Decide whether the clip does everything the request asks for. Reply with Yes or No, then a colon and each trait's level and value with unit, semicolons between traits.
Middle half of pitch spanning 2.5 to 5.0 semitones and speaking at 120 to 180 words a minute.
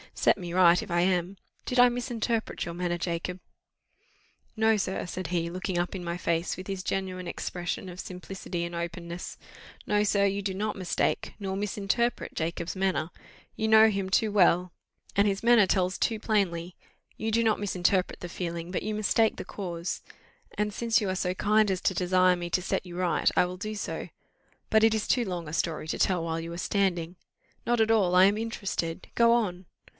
No: average, 3.2 semitones; average, 200 wpm